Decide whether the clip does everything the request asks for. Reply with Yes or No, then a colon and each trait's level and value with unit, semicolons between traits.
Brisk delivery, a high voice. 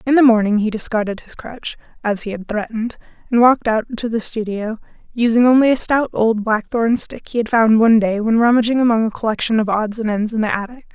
Yes: fast, 225 wpm; high, 225 Hz